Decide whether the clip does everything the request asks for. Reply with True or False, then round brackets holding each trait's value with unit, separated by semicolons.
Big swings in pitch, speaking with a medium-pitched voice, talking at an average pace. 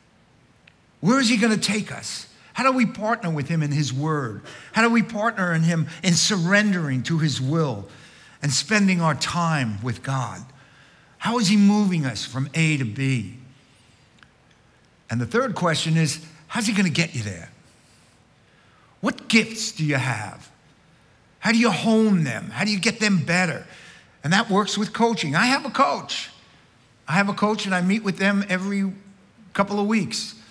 True (7.0 semitones; 175 Hz; 180 wpm)